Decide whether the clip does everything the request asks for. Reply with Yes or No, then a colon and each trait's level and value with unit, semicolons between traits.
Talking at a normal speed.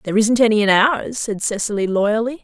Yes: average, 195 wpm